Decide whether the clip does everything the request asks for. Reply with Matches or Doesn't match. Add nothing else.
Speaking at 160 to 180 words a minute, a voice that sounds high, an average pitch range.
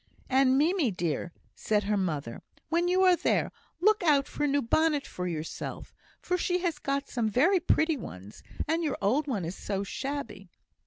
Doesn't match